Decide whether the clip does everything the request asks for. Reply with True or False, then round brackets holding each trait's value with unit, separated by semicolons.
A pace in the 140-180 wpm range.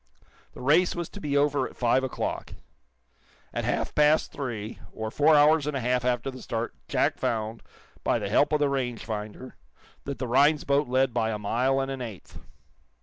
False (190 wpm)